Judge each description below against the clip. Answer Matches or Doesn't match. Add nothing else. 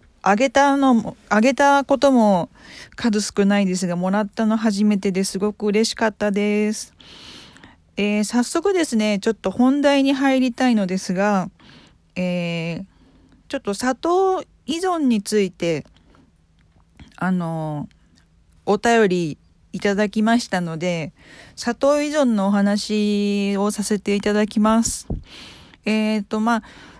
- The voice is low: Doesn't match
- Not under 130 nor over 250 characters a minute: Matches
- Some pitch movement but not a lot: Matches